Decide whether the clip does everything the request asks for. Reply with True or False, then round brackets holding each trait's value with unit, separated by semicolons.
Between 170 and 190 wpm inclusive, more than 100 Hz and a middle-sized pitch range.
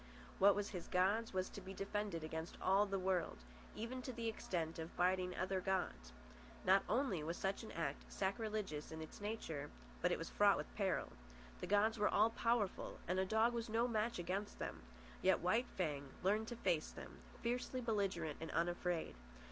True (180 wpm; 190 Hz; 4.5 semitones)